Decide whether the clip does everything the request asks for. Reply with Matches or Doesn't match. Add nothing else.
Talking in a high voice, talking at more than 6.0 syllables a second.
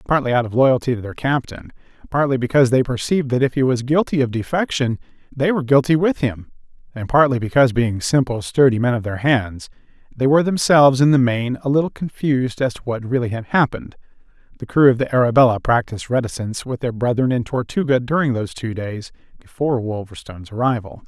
Doesn't match